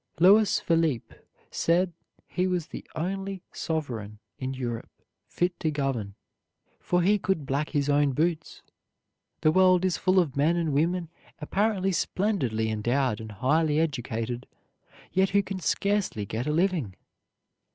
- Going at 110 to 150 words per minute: Yes, average, 140 wpm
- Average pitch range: No, wide, 6.0 semitones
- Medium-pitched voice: Yes, medium, 160 Hz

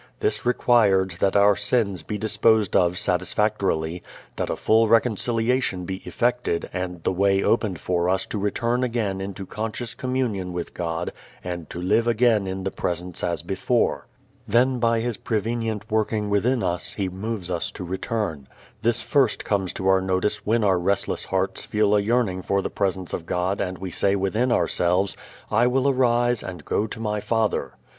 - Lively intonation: No, average, 3.7 semitones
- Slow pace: No, average, 175 wpm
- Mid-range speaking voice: No, low, 100 Hz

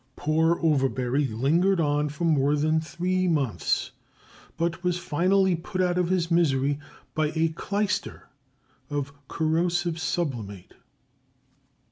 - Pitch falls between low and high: Yes, medium, 160 Hz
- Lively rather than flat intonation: No, average, 3.4 semitones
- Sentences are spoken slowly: Yes, slow, 115 wpm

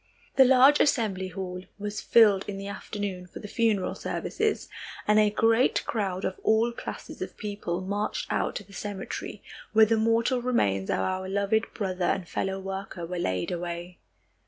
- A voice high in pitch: Yes, high, 200 Hz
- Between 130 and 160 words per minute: No, average, 170 wpm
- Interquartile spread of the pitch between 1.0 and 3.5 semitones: Yes, average, 3.1 semitones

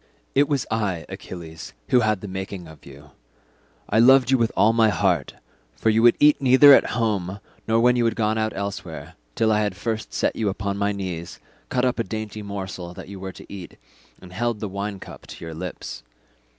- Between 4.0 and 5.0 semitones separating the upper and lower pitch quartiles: No, average, 3.4 semitones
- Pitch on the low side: Yes, low, 105 Hz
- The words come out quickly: Yes, fast, 210 wpm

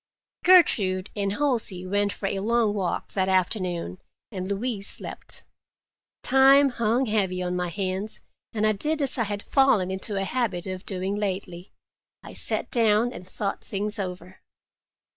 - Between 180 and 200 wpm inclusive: No, average, 150 wpm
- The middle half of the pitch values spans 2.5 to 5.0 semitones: Yes, average, 3.4 semitones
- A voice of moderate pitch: No, high, 200 Hz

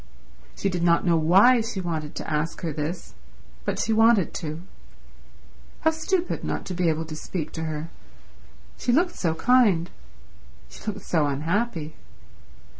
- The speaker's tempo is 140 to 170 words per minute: Yes, average, 155 wpm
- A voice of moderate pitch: Yes, medium, 170 Hz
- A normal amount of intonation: No, wide, 5.7 semitones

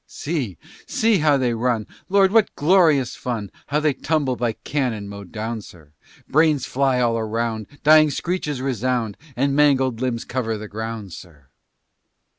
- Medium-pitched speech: No, low, 125 Hz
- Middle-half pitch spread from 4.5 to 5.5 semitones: Yes, average, 4.9 semitones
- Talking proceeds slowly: No, average, 150 wpm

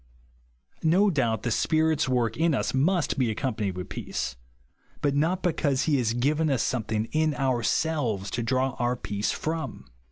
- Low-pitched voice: Yes, low, 130 Hz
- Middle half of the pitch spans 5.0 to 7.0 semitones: Yes, wide, 5.4 semitones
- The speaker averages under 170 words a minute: Yes, average, 160 wpm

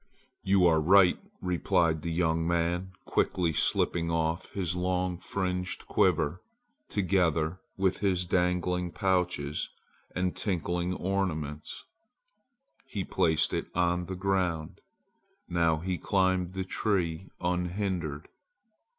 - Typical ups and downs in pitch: No, narrow, 1.9 semitones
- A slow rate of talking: Yes, slow, 105 wpm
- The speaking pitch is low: Yes, very low, 90 Hz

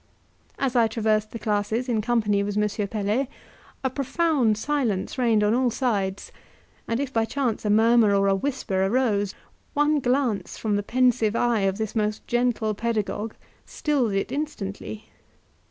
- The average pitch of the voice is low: No, high, 225 Hz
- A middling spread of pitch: Yes, average, 3.3 semitones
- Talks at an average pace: Yes, average, 155 wpm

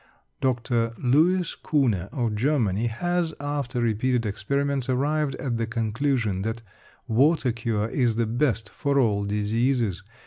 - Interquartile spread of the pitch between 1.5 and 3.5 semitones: No, average, 4.1 semitones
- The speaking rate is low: Yes, slow, 130 wpm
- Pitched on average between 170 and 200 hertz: No, low, 120 Hz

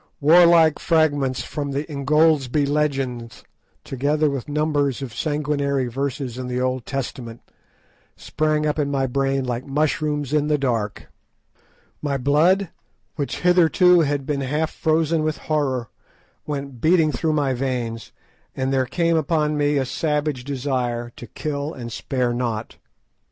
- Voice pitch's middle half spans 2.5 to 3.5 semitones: Yes, average, 2.9 semitones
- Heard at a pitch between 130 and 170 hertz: Yes, medium, 140 Hz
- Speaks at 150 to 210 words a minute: No, average, 140 wpm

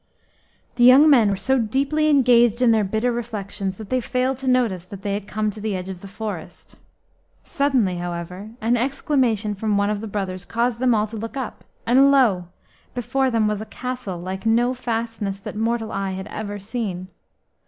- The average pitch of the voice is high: Yes, high, 220 Hz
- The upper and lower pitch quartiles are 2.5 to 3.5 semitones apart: No, average, 3.9 semitones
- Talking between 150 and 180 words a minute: No, average, 195 wpm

